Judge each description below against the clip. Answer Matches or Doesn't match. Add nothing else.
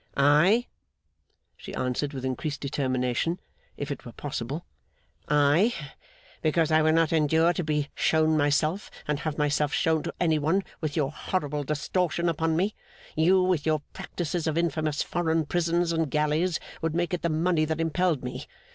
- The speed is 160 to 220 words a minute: Matches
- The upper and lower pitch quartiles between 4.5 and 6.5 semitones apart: Doesn't match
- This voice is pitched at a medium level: Matches